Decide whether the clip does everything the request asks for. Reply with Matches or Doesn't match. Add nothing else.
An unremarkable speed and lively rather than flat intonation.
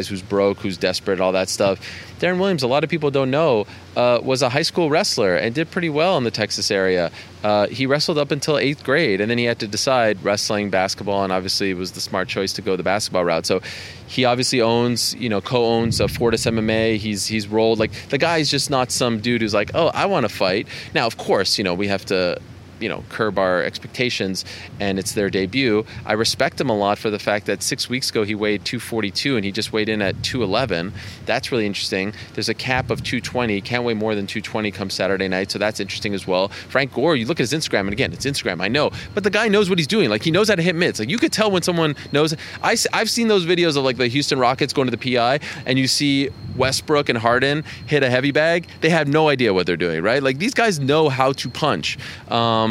Doesn't match